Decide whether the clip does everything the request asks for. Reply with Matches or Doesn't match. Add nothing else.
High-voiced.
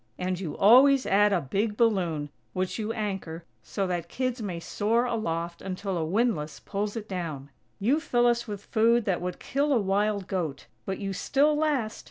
Matches